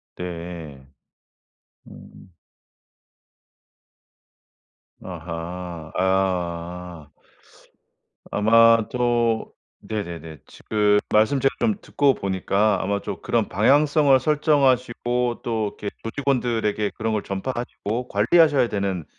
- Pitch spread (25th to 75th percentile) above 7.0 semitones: No, wide, 5.4 semitones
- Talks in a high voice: No, low, 105 Hz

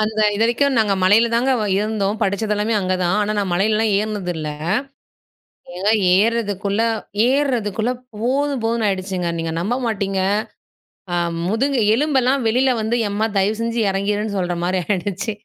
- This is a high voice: Yes, high, 215 Hz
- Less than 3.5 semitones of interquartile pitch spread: Yes, average, 3.0 semitones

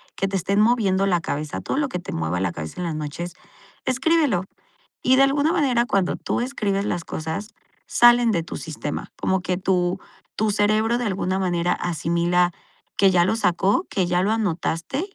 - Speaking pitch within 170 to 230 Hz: Yes, high, 190 Hz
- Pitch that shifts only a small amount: No, average, 4.6 semitones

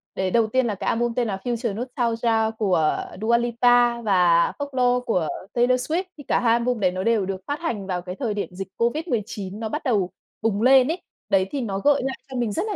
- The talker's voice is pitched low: No, high, 230 Hz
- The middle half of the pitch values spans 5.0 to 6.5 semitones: No, average, 4.0 semitones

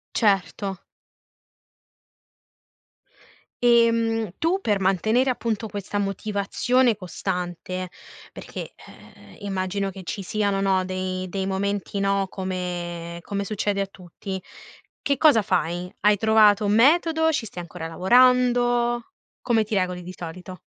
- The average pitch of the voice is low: No, high, 200 Hz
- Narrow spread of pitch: No, average, 3.5 semitones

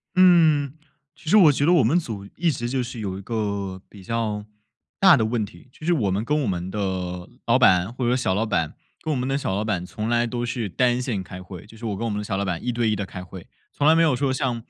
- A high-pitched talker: No, low, 115 Hz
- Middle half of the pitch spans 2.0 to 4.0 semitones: No, average, 5.2 semitones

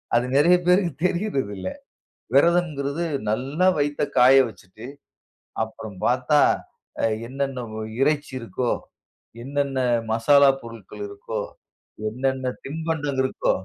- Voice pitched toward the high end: No, medium, 140 Hz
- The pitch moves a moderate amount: Yes, average, 3.8 semitones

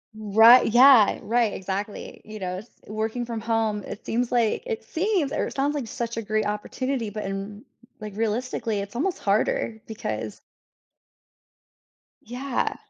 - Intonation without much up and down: No, average, 3.0 semitones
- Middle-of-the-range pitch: No, high, 225 Hz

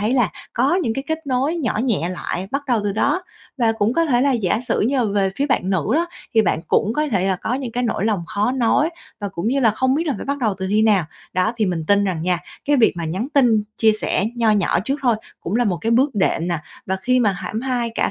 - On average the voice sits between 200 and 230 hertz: Yes, high, 225 Hz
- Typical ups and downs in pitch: Yes, average, 5.0 semitones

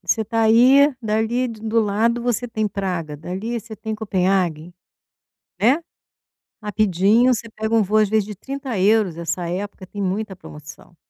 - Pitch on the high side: Yes, high, 215 Hz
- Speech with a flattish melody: No, average, 3.2 semitones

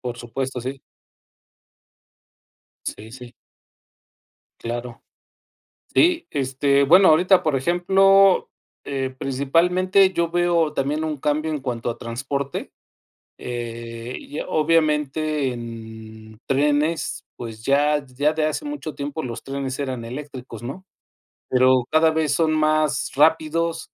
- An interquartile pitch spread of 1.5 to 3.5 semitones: No, average, 3.9 semitones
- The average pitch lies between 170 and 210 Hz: No, medium, 140 Hz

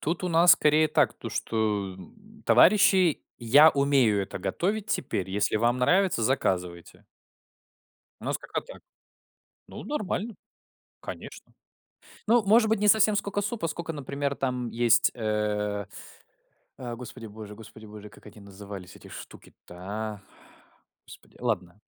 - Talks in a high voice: No, low, 120 Hz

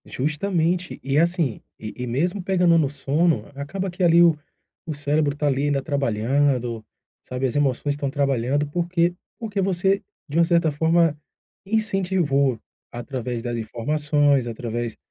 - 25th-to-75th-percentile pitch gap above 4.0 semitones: Yes, average, 4.5 semitones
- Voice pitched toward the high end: No, medium, 145 Hz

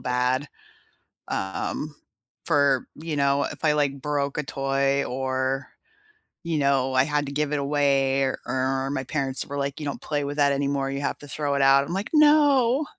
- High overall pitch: No, medium, 140 Hz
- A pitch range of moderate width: No, narrow, 1.5 semitones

